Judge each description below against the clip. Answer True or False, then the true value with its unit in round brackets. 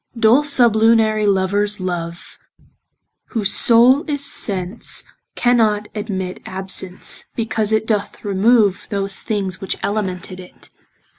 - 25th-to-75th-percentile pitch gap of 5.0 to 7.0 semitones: False (3.0 semitones)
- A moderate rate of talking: False (105 wpm)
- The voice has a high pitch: True (210 Hz)